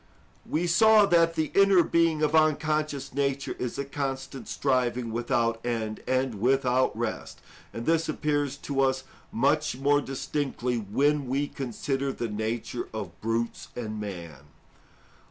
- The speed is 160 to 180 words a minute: No, slow, 135 wpm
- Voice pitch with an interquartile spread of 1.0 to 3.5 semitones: No, average, 4.1 semitones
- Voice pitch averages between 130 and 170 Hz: Yes, low, 135 Hz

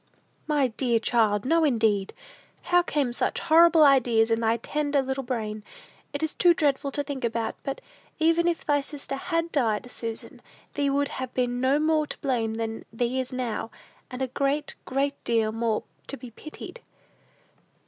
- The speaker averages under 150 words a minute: No, average, 175 wpm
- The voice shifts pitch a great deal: No, average, 4.1 semitones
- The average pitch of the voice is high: Yes, very high, 265 Hz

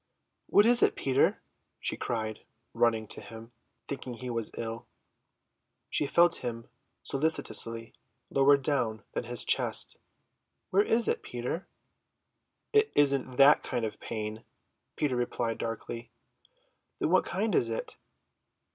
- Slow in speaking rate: Yes, slow, 130 wpm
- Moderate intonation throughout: Yes, average, 4.1 semitones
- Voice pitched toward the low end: Yes, low, 125 Hz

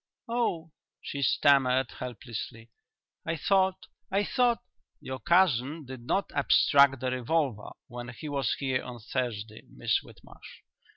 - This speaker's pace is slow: Yes, slow, 130 wpm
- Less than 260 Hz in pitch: Yes, low, 135 Hz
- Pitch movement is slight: No, average, 5.0 semitones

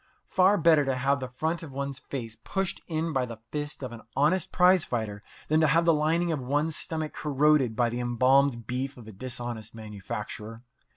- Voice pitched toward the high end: No, medium, 140 Hz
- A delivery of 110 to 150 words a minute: No, average, 195 wpm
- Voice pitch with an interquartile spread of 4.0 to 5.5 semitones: Yes, average, 4.7 semitones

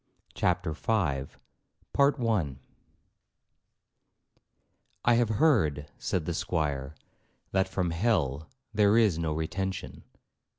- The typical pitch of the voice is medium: No, very low, 90 Hz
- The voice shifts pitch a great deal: Yes, wide, 6.0 semitones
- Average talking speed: No, slow, 85 wpm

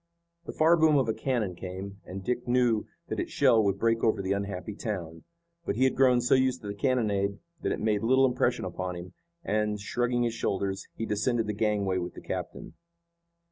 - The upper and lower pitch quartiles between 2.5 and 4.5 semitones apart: Yes, average, 3.8 semitones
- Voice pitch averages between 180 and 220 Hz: No, low, 105 Hz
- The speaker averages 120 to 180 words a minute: No, fast, 205 wpm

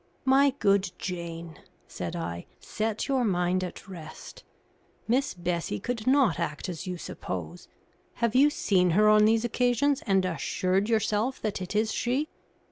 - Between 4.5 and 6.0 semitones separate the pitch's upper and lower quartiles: Yes, average, 5.2 semitones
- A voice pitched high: Yes, high, 205 Hz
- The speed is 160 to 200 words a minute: No, average, 150 wpm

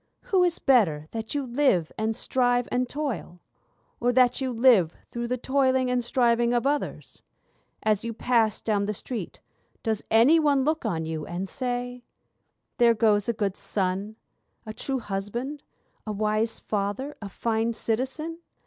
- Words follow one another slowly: No, average, 160 wpm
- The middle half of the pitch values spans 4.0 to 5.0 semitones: No, average, 3.5 semitones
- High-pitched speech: Yes, high, 235 Hz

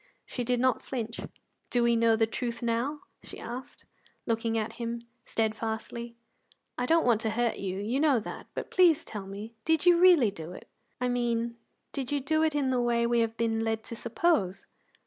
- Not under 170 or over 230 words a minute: Yes, average, 195 wpm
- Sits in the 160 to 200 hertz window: No, high, 235 Hz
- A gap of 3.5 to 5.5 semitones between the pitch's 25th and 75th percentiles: No, narrow, 2.4 semitones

